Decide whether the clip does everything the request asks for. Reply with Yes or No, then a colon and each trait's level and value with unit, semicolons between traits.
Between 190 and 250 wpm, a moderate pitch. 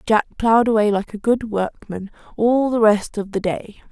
No: average, 200 wpm; high, 215 Hz